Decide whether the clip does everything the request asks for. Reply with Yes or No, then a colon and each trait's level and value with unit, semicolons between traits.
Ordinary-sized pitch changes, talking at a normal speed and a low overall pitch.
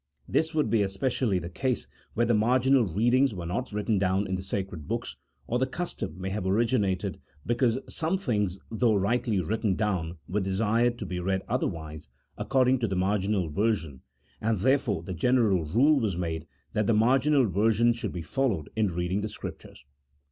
Yes: average, 4.5 semitones; average, 185 wpm; low, 105 Hz